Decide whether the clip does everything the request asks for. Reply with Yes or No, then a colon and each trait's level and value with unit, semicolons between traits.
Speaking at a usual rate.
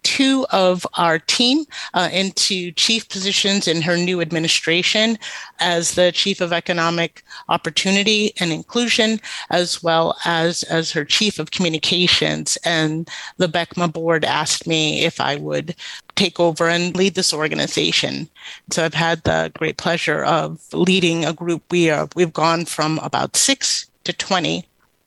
Yes: average, 150 wpm